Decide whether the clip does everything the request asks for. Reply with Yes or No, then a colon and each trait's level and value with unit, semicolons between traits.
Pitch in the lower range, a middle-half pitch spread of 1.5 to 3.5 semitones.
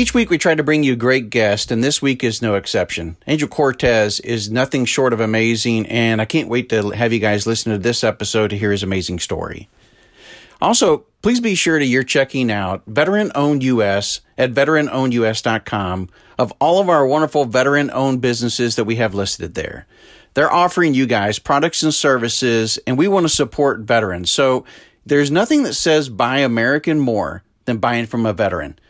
No: low, 120 Hz; average, 4.7 semitones